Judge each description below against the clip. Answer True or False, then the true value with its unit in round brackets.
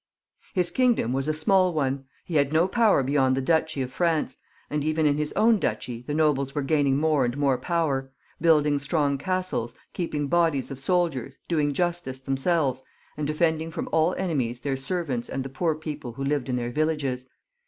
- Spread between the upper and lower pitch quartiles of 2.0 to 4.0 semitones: True (3.5 semitones)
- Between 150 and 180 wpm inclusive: False (190 wpm)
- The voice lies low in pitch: False (150 Hz)